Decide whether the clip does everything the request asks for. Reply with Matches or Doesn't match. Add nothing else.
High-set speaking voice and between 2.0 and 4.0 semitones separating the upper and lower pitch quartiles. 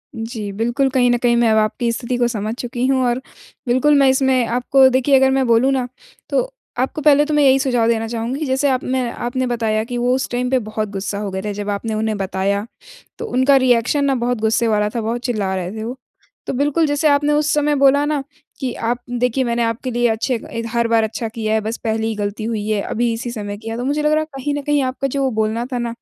Matches